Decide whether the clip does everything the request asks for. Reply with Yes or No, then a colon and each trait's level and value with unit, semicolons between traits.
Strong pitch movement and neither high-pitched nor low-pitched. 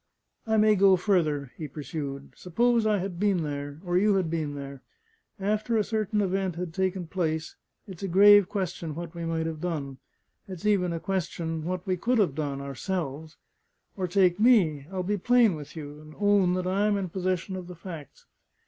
No: average, 4.0 semitones; medium, 180 Hz